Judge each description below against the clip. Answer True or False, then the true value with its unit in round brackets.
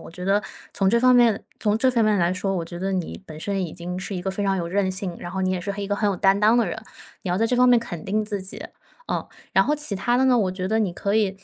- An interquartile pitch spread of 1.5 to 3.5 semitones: True (3.0 semitones)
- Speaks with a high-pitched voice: True (195 Hz)